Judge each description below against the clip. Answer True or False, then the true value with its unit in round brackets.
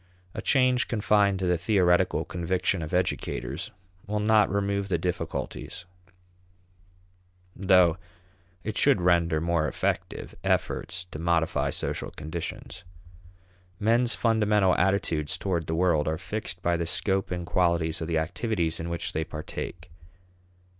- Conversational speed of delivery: False (130 wpm)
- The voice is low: True (90 Hz)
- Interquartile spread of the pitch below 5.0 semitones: True (3.3 semitones)